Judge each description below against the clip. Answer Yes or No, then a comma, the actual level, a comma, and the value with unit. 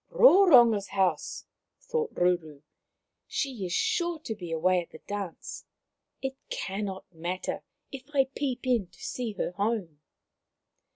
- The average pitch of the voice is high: Yes, high, 205 Hz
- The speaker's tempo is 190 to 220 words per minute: No, average, 150 wpm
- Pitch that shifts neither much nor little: No, wide, 6.9 semitones